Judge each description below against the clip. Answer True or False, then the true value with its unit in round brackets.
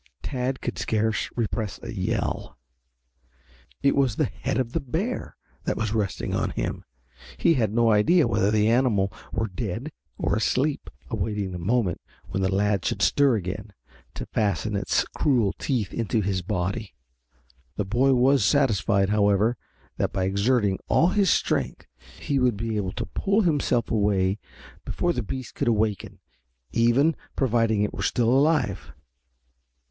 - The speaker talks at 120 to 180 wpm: True (155 wpm)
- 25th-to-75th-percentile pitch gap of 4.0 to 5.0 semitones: True (4.4 semitones)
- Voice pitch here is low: True (110 Hz)